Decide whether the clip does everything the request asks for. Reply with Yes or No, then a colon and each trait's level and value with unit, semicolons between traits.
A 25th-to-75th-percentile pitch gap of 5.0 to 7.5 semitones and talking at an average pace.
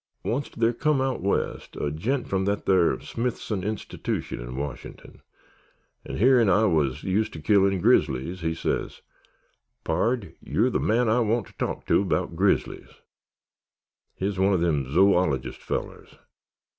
Yes: wide, 5.5 semitones; average, 150 wpm